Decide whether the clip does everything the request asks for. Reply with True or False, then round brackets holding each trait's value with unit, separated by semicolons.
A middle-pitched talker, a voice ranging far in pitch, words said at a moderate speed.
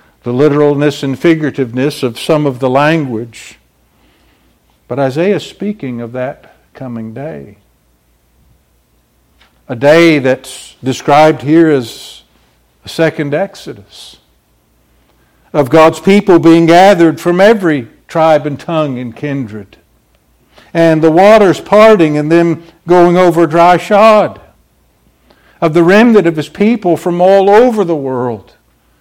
False (145 Hz; 7.3 semitones; 120 wpm)